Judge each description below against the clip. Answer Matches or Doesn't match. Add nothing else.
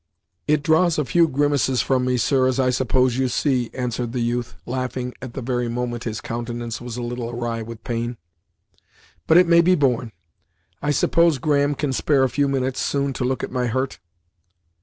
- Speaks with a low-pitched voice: Matches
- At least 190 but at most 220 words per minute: Matches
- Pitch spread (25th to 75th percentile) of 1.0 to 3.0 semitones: Matches